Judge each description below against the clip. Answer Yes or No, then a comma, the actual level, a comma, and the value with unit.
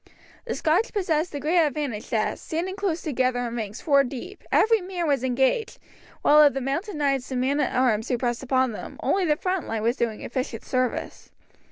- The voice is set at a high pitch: Yes, very high, 275 Hz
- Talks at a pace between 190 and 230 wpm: Yes, average, 200 wpm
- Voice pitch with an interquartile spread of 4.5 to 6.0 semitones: Yes, wide, 5.4 semitones